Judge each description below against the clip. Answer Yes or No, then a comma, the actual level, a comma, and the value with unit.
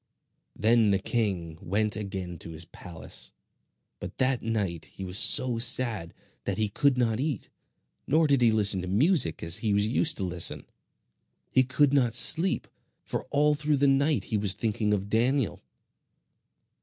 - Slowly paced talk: No, average, 165 wpm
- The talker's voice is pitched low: Yes, low, 110 Hz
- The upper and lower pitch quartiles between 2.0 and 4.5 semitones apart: No, average, 5.3 semitones